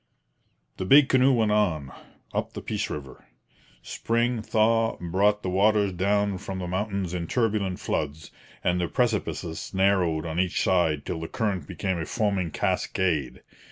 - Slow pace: No, average, 155 wpm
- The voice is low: Yes, very low, 95 Hz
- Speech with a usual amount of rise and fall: Yes, average, 3.7 semitones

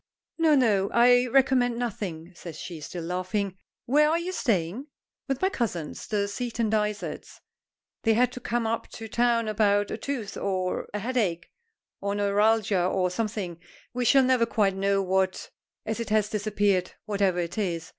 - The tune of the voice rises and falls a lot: No, average, 4.0 semitones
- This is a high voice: Yes, high, 210 Hz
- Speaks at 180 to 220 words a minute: No, average, 165 wpm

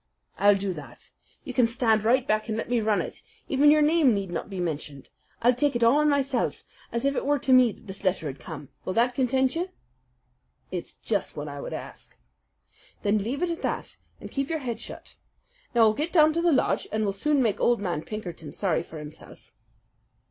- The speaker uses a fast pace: Yes, fast, 220 wpm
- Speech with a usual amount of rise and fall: No, wide, 5.9 semitones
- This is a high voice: Yes, high, 230 Hz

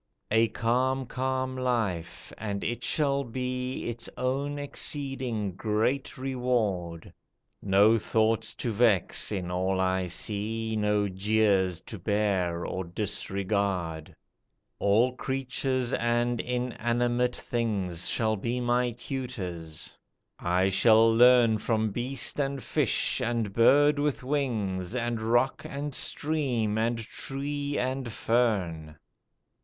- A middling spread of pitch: Yes, average, 4.1 semitones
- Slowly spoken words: Yes, slow, 110 wpm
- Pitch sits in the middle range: No, low, 115 Hz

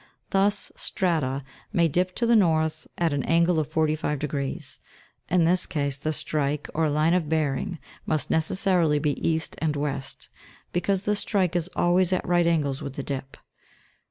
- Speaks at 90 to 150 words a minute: No, average, 170 wpm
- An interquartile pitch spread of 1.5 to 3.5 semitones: Yes, average, 3.2 semitones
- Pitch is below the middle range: No, medium, 160 Hz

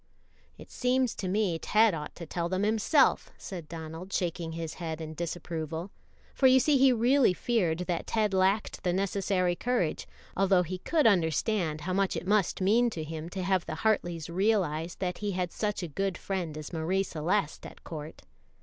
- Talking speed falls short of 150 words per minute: No, average, 185 wpm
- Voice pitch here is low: No, medium, 185 Hz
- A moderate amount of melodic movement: Yes, average, 4.0 semitones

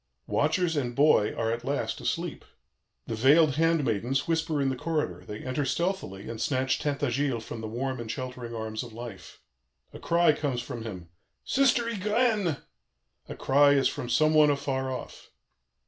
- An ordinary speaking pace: Yes, average, 165 wpm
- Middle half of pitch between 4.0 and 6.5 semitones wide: Yes, average, 4.8 semitones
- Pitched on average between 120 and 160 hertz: Yes, low, 135 Hz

